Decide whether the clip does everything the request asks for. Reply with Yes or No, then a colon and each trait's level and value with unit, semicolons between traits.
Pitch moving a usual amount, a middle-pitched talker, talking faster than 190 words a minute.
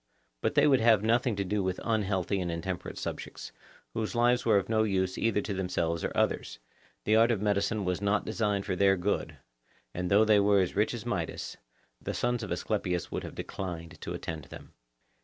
No: average, 3.1 semitones; low, 100 Hz; average, 200 wpm